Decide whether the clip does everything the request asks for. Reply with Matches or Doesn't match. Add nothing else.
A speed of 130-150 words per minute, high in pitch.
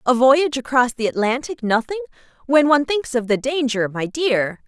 Doesn't match